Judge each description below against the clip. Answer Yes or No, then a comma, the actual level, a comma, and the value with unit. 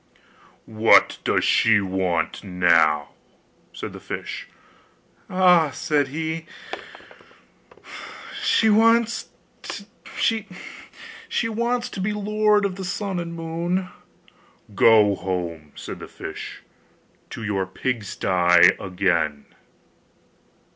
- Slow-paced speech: Yes, slow, 85 wpm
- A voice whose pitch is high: No, medium, 160 Hz